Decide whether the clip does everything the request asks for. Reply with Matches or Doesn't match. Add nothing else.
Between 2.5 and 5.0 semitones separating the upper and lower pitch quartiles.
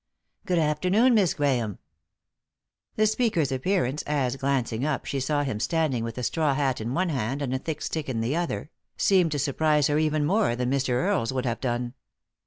Matches